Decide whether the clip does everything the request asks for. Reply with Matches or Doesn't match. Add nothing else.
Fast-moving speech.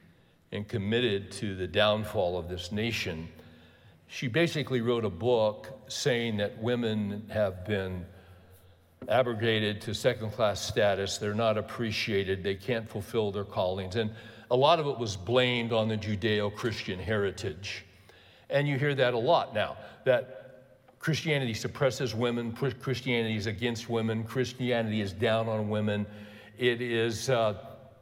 Doesn't match